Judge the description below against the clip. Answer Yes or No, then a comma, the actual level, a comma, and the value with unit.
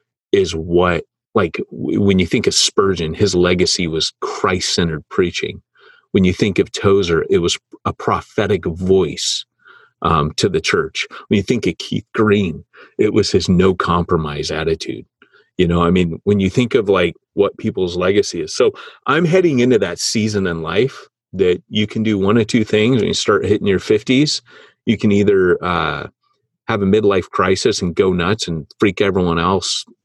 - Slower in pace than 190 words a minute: Yes, average, 175 wpm